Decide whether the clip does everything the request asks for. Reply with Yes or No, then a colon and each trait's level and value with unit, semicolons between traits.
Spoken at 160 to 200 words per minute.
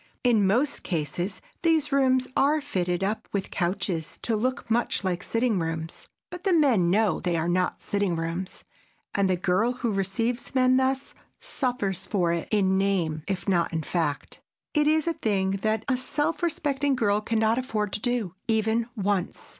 Yes: average, 175 wpm